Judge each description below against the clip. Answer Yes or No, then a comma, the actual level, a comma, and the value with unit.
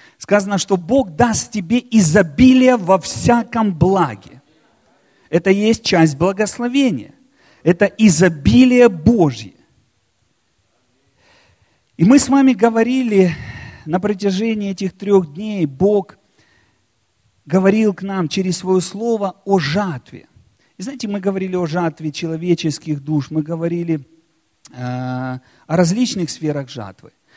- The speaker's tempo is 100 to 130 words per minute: Yes, average, 110 wpm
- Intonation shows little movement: No, average, 5.2 semitones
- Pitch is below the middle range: No, high, 190 Hz